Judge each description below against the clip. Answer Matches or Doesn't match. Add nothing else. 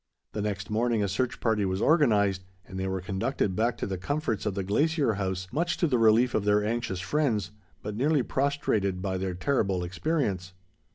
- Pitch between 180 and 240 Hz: Doesn't match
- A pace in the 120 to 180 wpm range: Doesn't match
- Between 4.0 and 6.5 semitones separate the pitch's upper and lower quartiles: Matches